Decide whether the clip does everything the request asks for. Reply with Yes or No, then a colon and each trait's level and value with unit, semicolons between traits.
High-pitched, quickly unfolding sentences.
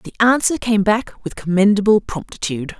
No: high, 205 Hz; average, 150 wpm